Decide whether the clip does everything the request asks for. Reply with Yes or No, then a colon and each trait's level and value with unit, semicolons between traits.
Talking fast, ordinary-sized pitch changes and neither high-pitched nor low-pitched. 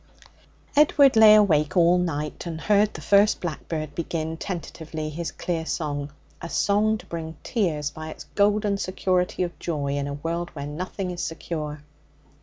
No: average, 160 wpm; average, 4.3 semitones; medium, 170 Hz